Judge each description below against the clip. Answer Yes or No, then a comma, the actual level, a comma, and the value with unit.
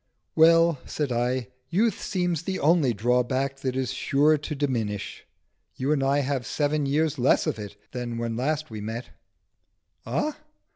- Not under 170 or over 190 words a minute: No, average, 155 wpm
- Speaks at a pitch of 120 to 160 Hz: Yes, low, 135 Hz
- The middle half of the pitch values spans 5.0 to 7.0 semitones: No, average, 4.0 semitones